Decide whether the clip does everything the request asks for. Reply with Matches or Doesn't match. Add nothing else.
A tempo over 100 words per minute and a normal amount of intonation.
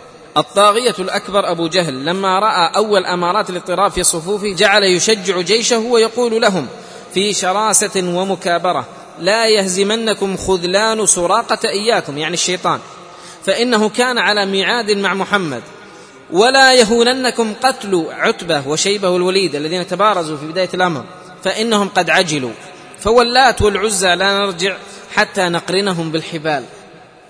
Matches